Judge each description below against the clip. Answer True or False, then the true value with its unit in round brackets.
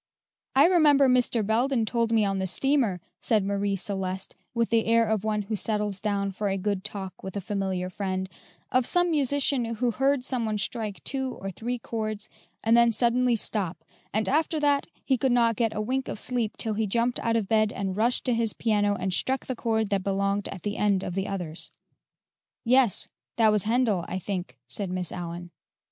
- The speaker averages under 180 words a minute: False (200 wpm)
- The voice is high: True (215 Hz)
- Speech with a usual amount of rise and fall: True (3.6 semitones)